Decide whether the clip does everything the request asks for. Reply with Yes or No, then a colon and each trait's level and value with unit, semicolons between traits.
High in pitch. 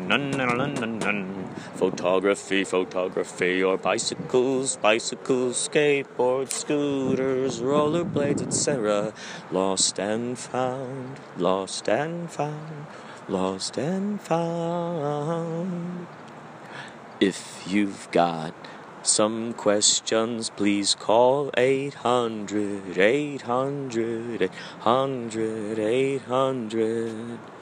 No: low, 125 Hz